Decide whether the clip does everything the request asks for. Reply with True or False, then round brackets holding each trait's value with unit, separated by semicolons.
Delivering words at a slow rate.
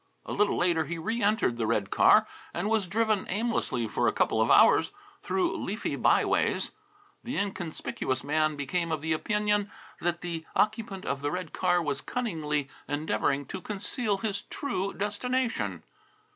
False (160 wpm)